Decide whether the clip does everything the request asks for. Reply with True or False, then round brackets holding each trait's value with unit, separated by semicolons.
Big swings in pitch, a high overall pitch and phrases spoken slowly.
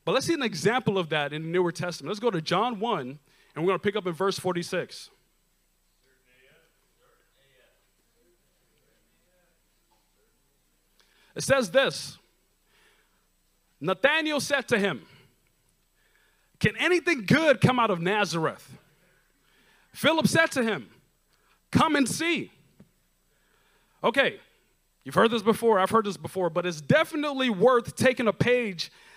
True (6.5 semitones; 210 Hz; 130 wpm)